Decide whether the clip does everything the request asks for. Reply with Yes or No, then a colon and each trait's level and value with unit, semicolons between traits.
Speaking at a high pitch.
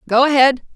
Yes: very high, 265 Hz